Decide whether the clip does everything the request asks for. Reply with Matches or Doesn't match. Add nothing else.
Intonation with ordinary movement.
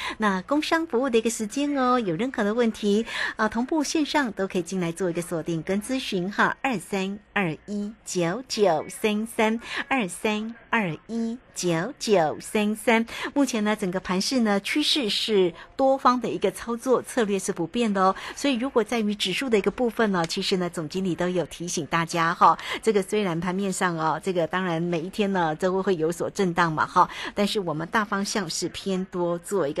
Matches